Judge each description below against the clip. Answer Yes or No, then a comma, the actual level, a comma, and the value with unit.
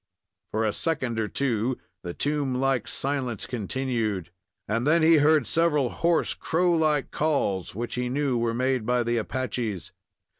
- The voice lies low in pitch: Yes, low, 130 Hz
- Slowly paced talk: No, average, 155 wpm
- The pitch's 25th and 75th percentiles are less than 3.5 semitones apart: No, average, 4.3 semitones